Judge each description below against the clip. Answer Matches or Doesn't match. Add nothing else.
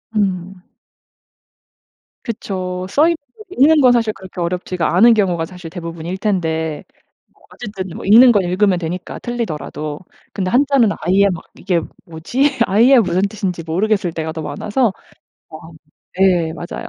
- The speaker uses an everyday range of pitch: Matches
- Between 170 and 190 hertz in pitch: Matches